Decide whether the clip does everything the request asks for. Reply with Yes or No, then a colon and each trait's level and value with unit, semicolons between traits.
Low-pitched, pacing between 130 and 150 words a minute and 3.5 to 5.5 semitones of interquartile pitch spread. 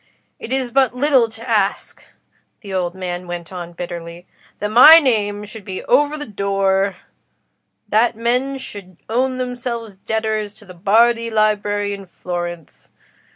No: high, 210 Hz; average, 140 wpm; average, 4.0 semitones